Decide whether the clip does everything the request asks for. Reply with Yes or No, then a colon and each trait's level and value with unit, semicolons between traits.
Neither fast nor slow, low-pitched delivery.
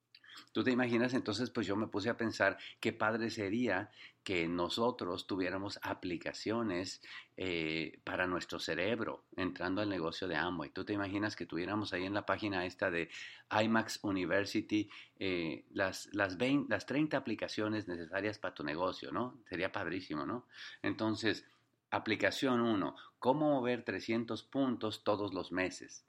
Yes: average, 145 wpm; low, 110 Hz